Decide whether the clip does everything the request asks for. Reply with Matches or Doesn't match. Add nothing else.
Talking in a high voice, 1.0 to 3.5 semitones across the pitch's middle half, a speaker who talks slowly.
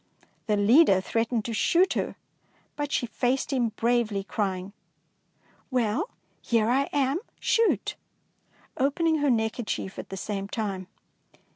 Doesn't match